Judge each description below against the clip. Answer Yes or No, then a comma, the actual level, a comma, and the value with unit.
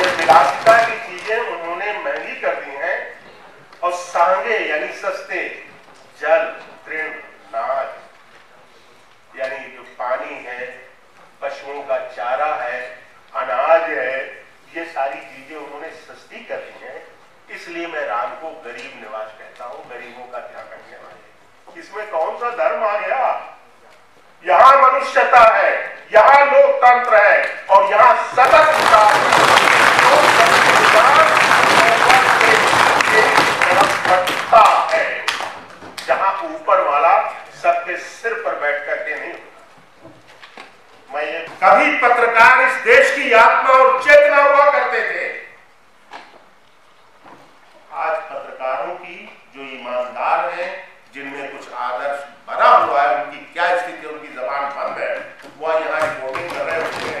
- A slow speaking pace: Yes, slow, 120 wpm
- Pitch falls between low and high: Yes, medium, 170 Hz